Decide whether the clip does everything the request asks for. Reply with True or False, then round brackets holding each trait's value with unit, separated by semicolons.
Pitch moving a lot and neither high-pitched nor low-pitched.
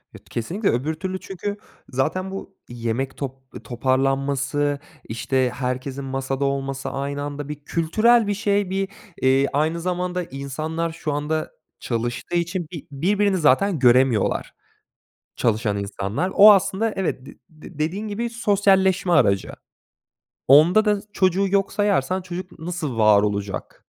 True (6.1 semitones; 155 Hz)